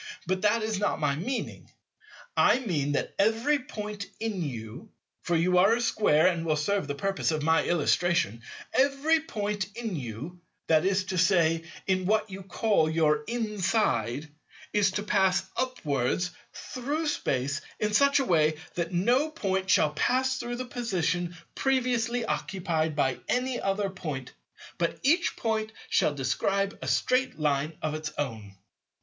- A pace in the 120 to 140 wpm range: No, average, 150 wpm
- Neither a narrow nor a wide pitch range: No, wide, 6.4 semitones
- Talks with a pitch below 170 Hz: No, high, 190 Hz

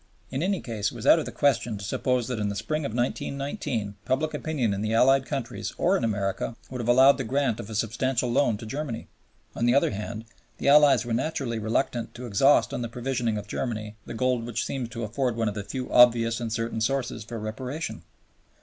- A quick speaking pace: Yes, fast, 220 wpm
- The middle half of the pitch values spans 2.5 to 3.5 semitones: Yes, average, 3.2 semitones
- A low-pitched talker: Yes, low, 120 Hz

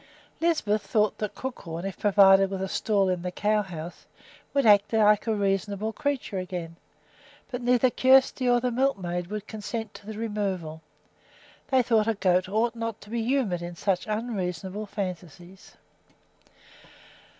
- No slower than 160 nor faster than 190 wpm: No, average, 150 wpm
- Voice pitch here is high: Yes, high, 210 Hz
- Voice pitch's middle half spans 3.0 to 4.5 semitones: Yes, average, 3.5 semitones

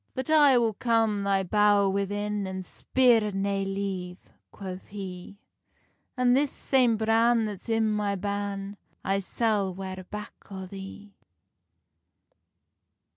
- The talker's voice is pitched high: Yes, high, 205 Hz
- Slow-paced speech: Yes, slow, 125 wpm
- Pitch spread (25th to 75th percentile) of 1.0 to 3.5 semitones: Yes, narrow, 2.5 semitones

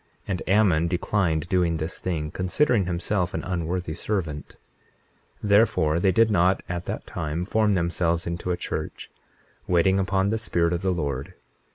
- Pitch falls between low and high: No, very low, 90 Hz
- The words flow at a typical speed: Yes, average, 160 wpm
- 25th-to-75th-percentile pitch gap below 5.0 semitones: Yes, narrow, 2.5 semitones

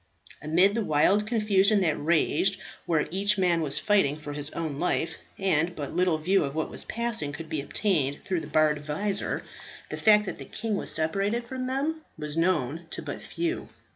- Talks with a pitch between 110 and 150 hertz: No, medium, 180 Hz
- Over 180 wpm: Yes, average, 190 wpm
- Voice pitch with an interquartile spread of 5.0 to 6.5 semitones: Yes, average, 5.3 semitones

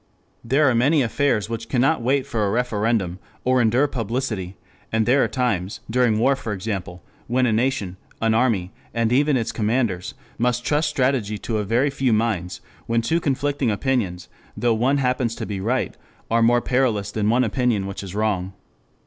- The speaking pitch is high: No, low, 115 Hz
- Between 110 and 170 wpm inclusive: No, average, 180 wpm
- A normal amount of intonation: Yes, average, 3.4 semitones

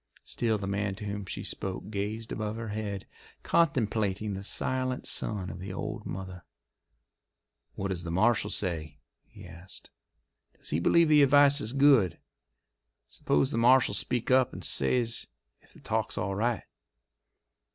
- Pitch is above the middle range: No, low, 105 Hz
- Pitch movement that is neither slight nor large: Yes, average, 4.1 semitones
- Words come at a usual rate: Yes, average, 150 wpm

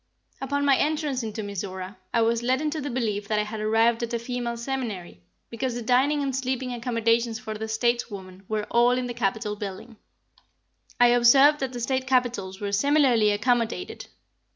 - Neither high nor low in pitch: No, high, 235 Hz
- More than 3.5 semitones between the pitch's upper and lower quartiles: No, average, 3.2 semitones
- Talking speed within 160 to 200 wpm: Yes, average, 175 wpm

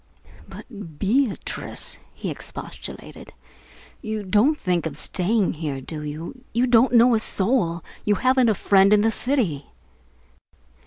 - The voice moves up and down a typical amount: No, wide, 6.0 semitones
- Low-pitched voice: No, high, 210 Hz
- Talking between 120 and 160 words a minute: Yes, average, 140 wpm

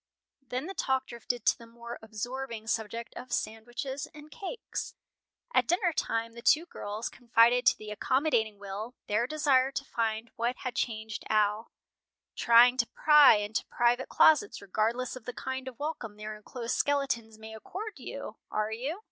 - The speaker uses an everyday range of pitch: Yes, average, 3.3 semitones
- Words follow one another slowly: No, average, 165 wpm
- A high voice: Yes, high, 240 Hz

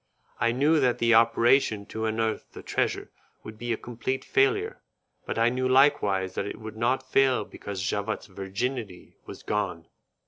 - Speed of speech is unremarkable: Yes, average, 165 wpm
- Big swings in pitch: No, average, 3.3 semitones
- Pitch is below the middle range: Yes, low, 115 Hz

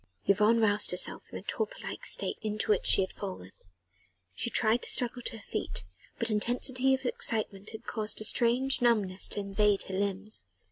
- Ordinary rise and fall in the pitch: Yes, average, 3.0 semitones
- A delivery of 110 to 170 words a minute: No, average, 185 wpm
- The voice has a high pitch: Yes, high, 215 Hz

